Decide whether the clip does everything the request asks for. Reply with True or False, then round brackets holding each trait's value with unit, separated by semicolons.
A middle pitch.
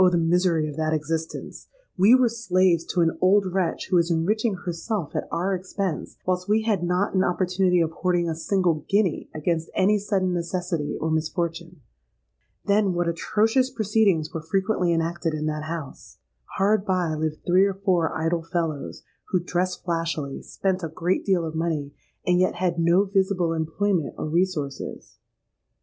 True (175 Hz)